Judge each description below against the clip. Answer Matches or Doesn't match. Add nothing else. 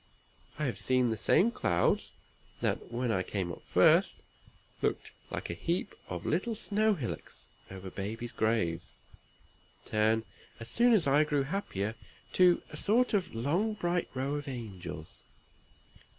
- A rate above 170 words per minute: Doesn't match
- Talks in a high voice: Doesn't match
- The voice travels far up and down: Matches